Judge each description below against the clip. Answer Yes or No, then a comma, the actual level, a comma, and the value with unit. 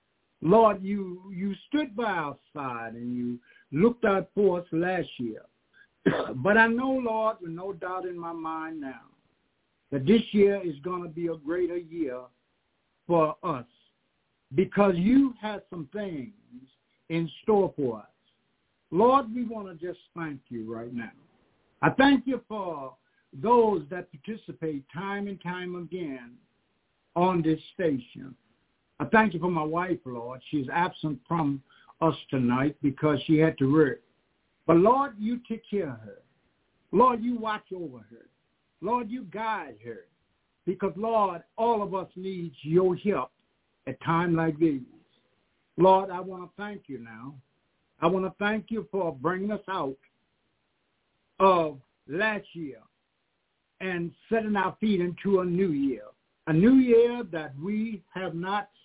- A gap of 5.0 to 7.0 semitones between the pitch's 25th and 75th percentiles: Yes, average, 5.3 semitones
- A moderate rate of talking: Yes, average, 150 wpm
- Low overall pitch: No, medium, 180 Hz